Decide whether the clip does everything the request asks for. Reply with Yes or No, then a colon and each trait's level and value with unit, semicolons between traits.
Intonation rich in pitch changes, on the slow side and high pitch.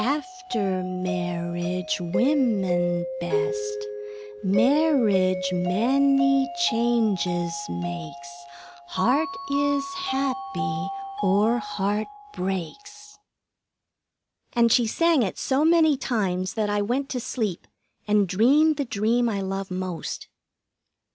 Yes: wide, 6.8 semitones; slow, 95 wpm; high, 205 Hz